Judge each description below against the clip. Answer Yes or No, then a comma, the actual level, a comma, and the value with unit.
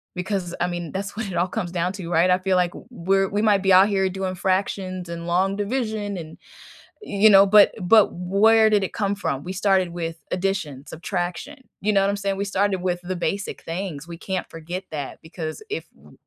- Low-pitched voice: No, high, 190 Hz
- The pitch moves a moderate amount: No, narrow, 2.3 semitones